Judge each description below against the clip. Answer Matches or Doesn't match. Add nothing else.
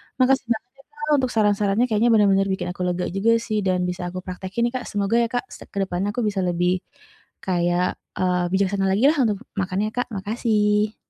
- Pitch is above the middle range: Matches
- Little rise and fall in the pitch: Doesn't match